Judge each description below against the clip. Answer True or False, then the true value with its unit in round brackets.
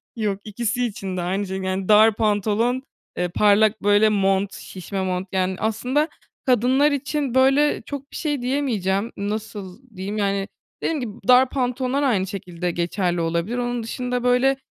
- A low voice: False (215 Hz)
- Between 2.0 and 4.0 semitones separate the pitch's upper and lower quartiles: False (4.6 semitones)